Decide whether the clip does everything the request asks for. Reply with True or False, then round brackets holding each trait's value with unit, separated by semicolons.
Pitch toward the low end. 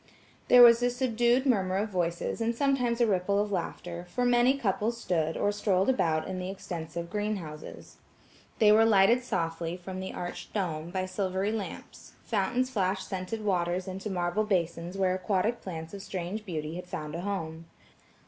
False (190 Hz)